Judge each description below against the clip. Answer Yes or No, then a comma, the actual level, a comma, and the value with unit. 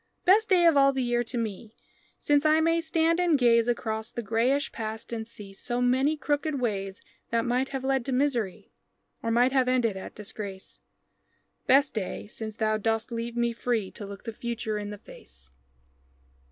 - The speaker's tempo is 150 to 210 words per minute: Yes, average, 185 wpm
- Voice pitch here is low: No, high, 235 Hz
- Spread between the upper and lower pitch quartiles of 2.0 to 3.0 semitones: No, average, 3.8 semitones